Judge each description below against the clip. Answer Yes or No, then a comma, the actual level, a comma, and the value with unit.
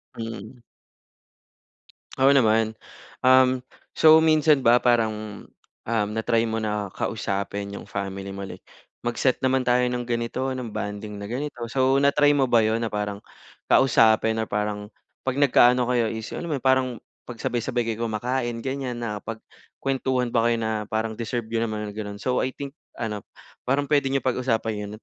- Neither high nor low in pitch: No, low, 115 Hz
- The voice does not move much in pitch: No, average, 3.1 semitones